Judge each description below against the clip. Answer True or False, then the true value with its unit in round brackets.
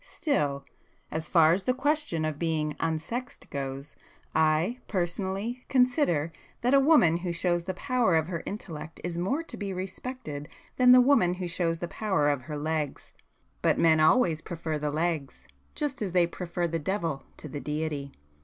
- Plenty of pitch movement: False (4.9 semitones)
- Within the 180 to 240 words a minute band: False (165 wpm)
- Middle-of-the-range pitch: True (170 Hz)